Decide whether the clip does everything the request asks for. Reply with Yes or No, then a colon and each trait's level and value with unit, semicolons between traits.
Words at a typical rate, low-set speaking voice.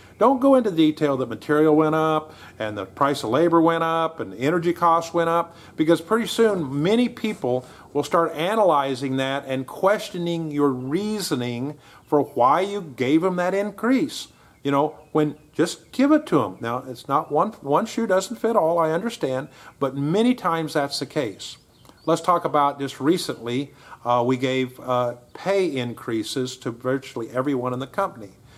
No: average, 175 wpm; medium, 150 Hz